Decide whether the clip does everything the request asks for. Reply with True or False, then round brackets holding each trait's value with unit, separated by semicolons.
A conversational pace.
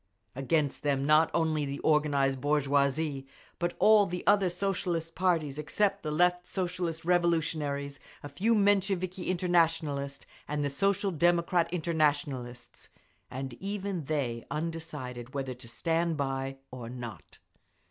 False (125 wpm)